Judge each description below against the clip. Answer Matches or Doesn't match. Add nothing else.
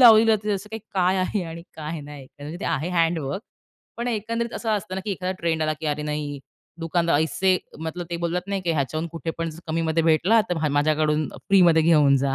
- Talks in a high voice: Doesn't match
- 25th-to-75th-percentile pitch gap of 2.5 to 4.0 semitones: Matches